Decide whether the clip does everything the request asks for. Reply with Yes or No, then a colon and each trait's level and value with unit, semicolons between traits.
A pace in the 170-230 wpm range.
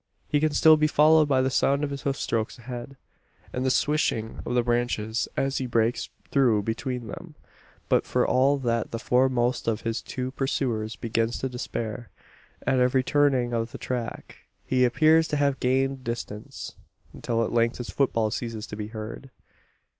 Yes: average, 175 wpm